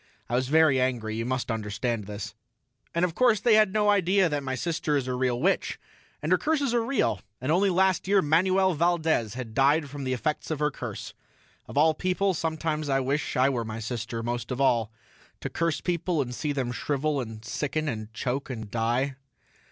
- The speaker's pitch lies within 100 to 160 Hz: Yes, medium, 140 Hz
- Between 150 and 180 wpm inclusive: No, fast, 205 wpm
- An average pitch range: No, wide, 5.8 semitones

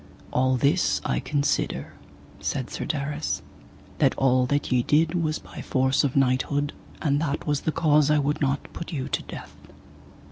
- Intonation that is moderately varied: No, narrow, 2.2 semitones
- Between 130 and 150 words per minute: No, average, 170 wpm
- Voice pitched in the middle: Yes, medium, 145 Hz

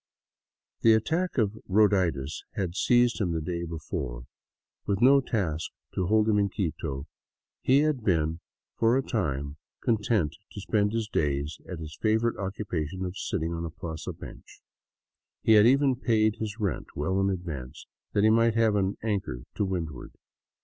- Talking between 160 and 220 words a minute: Yes, average, 165 wpm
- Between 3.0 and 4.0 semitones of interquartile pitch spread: No, average, 5.3 semitones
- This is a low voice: Yes, low, 100 Hz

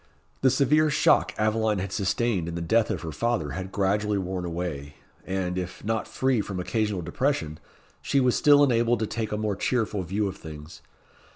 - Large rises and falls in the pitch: No, average, 4.5 semitones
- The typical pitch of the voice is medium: No, low, 105 Hz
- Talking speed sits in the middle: Yes, average, 185 wpm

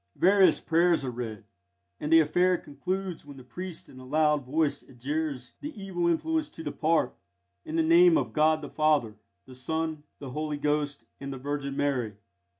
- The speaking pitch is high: No, medium, 150 Hz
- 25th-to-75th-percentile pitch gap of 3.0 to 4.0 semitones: Yes, average, 3.3 semitones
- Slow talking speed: No, average, 175 wpm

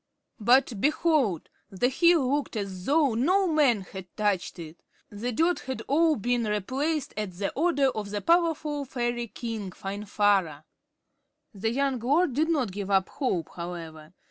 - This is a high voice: Yes, high, 240 Hz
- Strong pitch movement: Yes, wide, 6.6 semitones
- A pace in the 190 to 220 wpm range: No, average, 150 wpm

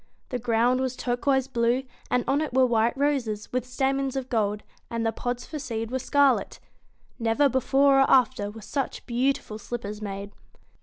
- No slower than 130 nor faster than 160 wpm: No, average, 200 wpm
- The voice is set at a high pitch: Yes, very high, 250 Hz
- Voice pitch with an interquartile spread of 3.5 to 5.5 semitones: No, average, 3.0 semitones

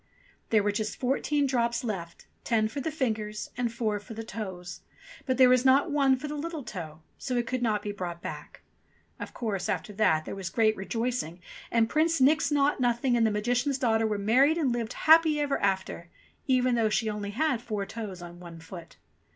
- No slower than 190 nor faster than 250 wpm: Yes, average, 200 wpm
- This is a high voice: Yes, high, 230 Hz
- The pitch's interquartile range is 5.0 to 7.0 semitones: No, average, 4.2 semitones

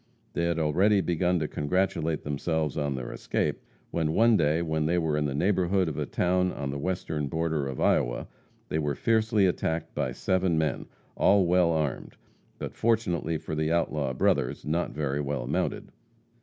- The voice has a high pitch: No, very low, 80 Hz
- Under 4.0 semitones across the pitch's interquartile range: Yes, average, 3.4 semitones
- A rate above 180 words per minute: No, average, 175 wpm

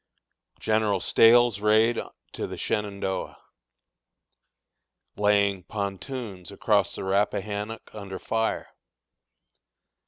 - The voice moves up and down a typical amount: No, narrow, 1.9 semitones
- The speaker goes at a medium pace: No, slow, 75 wpm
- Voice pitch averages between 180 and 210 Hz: No, low, 105 Hz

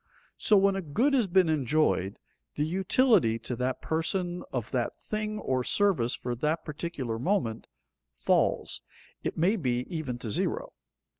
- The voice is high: No, medium, 160 Hz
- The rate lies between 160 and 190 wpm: No, average, 150 wpm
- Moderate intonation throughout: No, wide, 7.7 semitones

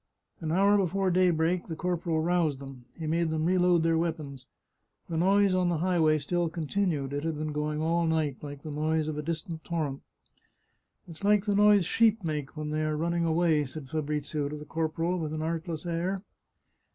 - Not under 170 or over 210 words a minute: Yes, average, 200 wpm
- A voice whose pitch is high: No, medium, 160 Hz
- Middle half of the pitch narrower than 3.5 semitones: Yes, narrow, 2.5 semitones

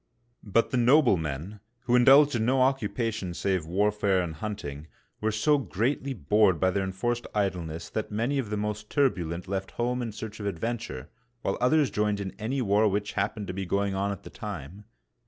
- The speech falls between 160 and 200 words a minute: Yes, average, 190 wpm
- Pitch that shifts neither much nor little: Yes, average, 3.9 semitones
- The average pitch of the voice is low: Yes, low, 105 Hz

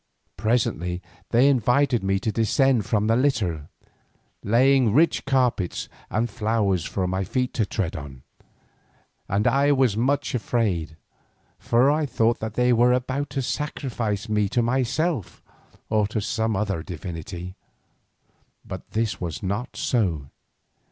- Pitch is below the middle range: Yes, low, 110 Hz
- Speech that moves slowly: Yes, slow, 130 wpm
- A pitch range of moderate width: Yes, average, 4.6 semitones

